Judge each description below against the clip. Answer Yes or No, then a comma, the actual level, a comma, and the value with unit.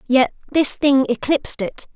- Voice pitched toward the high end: Yes, very high, 265 Hz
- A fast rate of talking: No, average, 155 wpm